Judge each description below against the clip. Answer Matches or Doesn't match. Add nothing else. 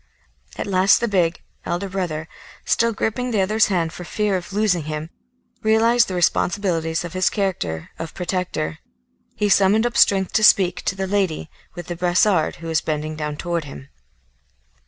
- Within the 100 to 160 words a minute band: Doesn't match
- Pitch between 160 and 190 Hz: Matches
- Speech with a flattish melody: Doesn't match